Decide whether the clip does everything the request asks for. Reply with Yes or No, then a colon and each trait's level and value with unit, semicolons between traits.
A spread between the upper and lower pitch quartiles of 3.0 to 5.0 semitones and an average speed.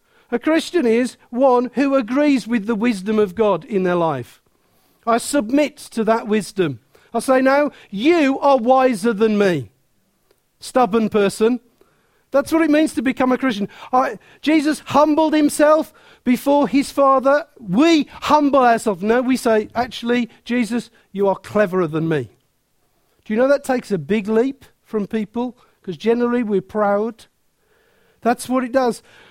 Yes: average, 4.5 semitones; average, 155 wpm